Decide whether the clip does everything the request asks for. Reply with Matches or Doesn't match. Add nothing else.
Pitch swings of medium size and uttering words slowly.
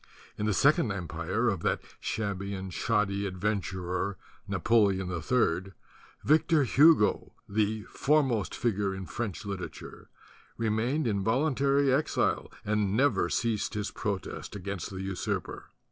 Matches